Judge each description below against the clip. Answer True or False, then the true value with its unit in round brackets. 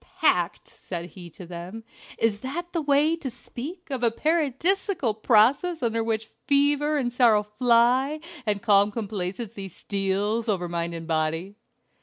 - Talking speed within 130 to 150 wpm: True (145 wpm)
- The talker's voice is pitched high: True (230 Hz)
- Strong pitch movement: True (6.0 semitones)